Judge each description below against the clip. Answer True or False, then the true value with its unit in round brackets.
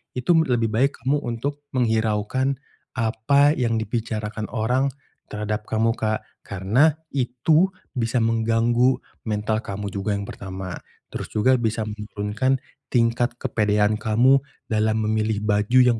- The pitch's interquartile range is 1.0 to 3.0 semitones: True (2.7 semitones)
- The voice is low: True (115 Hz)